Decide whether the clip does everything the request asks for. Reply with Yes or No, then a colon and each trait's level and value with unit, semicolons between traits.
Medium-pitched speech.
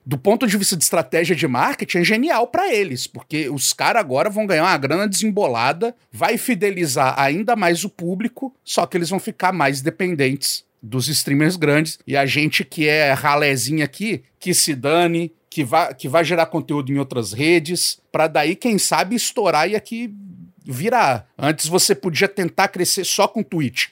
Yes: medium, 175 Hz